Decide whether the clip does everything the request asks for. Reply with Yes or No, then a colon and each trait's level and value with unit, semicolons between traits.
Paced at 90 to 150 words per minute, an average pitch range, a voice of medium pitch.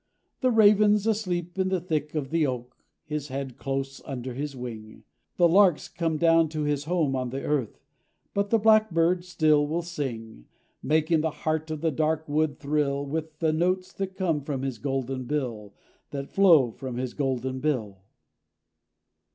No: average, 165 wpm; average, 4.1 semitones; medium, 150 Hz